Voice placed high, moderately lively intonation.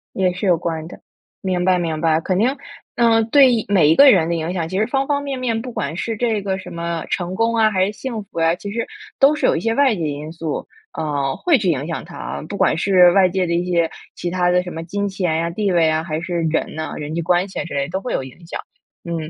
No: medium, 180 Hz; average, 4.6 semitones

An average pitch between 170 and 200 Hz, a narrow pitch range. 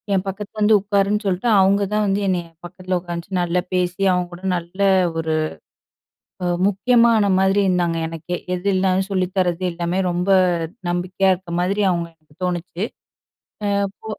Yes: medium, 185 Hz; narrow, 2.0 semitones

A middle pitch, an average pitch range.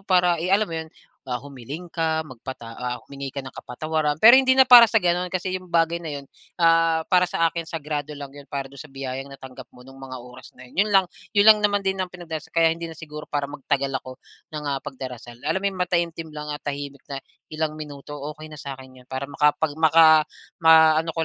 Yes: medium, 155 Hz; average, 3.5 semitones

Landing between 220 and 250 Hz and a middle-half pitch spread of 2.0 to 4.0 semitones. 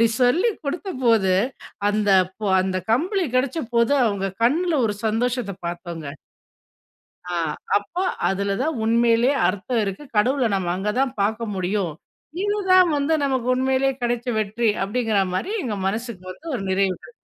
No: high, 235 Hz; average, 5.1 semitones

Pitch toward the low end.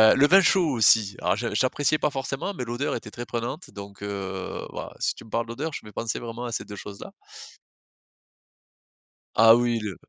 Yes: low, 115 Hz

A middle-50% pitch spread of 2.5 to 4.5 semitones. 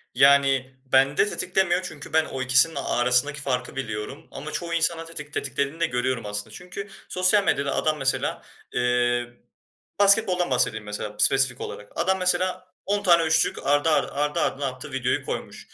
No: average, 4.9 semitones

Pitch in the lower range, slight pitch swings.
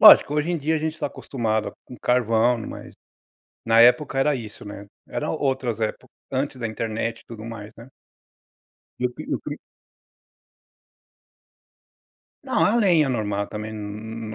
No: low, 115 Hz; average, 4.0 semitones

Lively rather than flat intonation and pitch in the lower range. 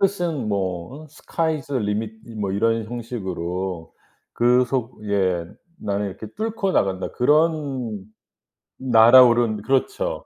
Yes: wide, 5.8 semitones; low, 115 Hz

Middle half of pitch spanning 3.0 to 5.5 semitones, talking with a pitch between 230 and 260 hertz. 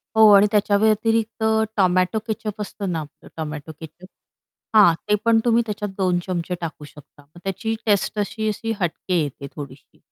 No: average, 4.7 semitones; high, 195 Hz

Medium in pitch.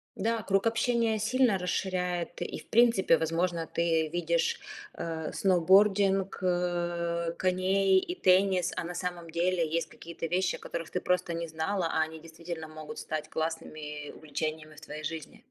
Yes: medium, 175 Hz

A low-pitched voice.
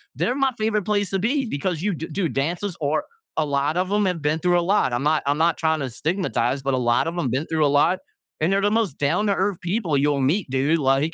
No: medium, 165 Hz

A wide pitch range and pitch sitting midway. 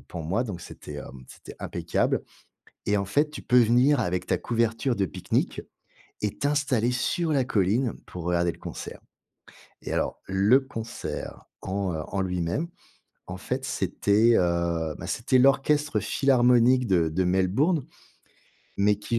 No: wide, 6.0 semitones; low, 110 Hz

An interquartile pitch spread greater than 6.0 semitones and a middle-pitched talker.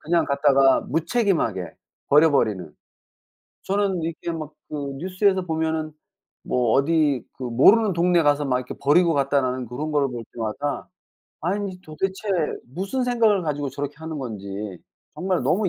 No: average, 5.3 semitones; medium, 155 Hz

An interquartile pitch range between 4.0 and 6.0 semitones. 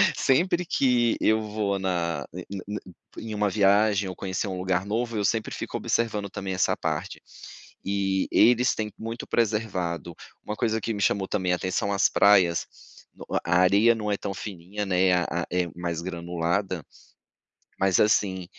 No: average, 2.9 semitones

